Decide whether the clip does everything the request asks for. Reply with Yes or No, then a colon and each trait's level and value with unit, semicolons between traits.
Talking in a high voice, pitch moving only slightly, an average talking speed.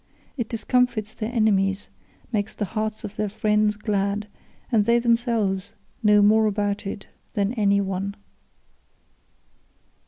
No: high, 210 Hz; narrow, 1.7 semitones; slow, 125 wpm